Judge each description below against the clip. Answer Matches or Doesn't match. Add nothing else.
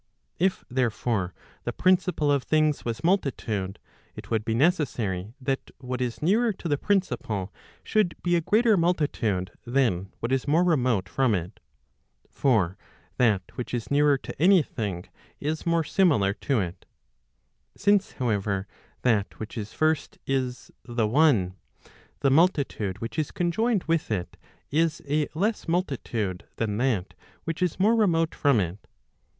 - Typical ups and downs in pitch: Doesn't match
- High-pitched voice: Doesn't match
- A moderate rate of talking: Matches